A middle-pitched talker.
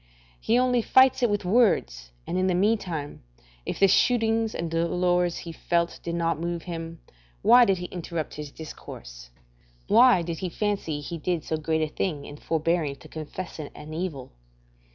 Yes: medium, 170 Hz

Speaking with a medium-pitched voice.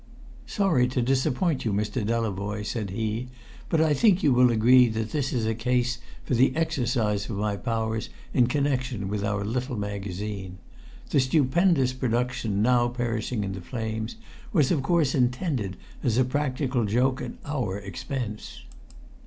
No: low, 120 Hz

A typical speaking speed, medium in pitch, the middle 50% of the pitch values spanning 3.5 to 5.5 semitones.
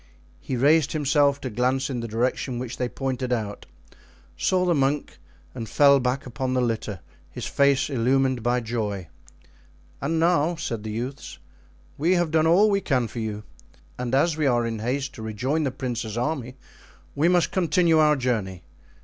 No: average, 175 wpm; low, 130 Hz; average, 3.9 semitones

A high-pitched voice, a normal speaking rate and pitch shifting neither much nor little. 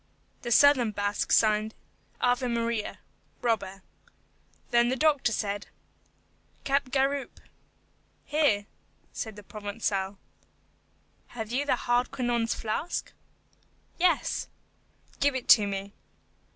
No: high, 235 Hz; slow, 85 wpm; average, 3.9 semitones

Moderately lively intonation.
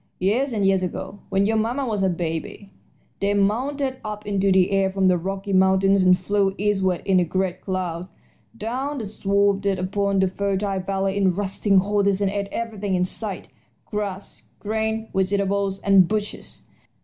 No: narrow, 1.5 semitones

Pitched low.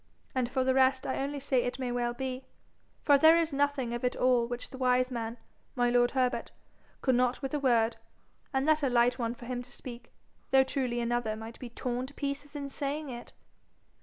No: very high, 255 Hz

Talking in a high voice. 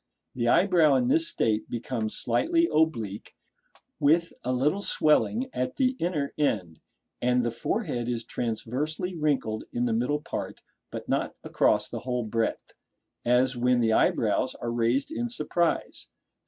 No: low, 125 Hz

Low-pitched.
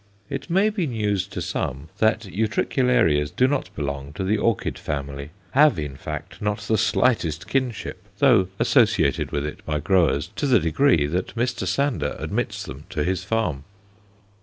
Yes: very low, 95 Hz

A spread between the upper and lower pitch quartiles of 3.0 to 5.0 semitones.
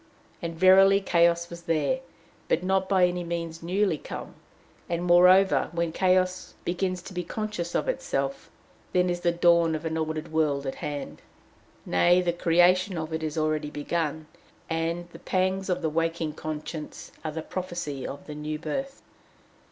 No: narrow, 2.6 semitones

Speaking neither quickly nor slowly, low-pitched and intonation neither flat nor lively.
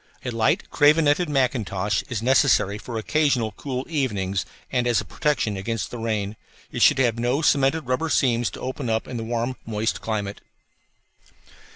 Yes: average, 165 wpm; low, 120 Hz; average, 3.6 semitones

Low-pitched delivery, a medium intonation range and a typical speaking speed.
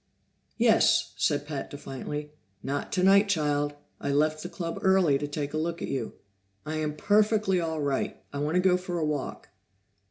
No: medium, 155 Hz; average, 3.7 semitones; average, 180 wpm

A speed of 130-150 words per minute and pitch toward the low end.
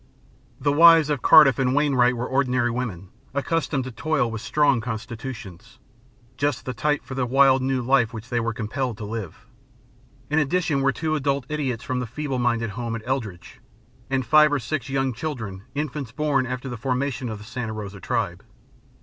No: average, 185 wpm; low, 130 Hz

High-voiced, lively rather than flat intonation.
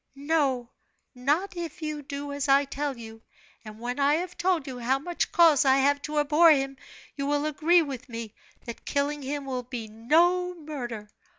No: very high, 285 Hz; average, 3.3 semitones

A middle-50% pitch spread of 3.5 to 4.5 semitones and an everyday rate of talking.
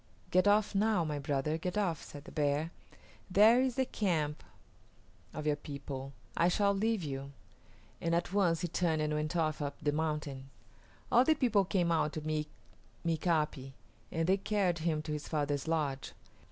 Yes: average, 4.1 semitones; average, 175 wpm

